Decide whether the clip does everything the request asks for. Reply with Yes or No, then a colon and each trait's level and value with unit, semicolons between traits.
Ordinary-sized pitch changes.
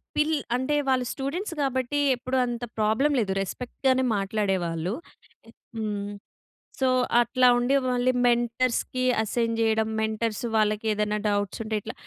Yes: average, 3.3 semitones